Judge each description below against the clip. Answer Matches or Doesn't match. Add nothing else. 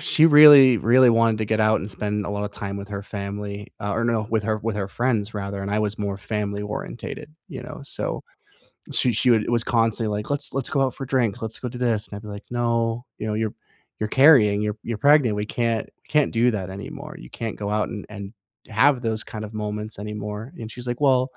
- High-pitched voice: Doesn't match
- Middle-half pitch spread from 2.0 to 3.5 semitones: Matches